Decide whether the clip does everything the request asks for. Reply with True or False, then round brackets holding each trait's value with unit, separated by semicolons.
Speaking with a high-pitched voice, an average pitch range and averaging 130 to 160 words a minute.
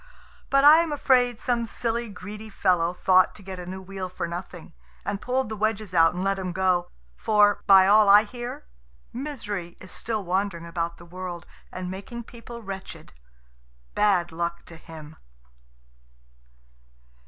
True (195 Hz; 3.6 semitones; 155 wpm)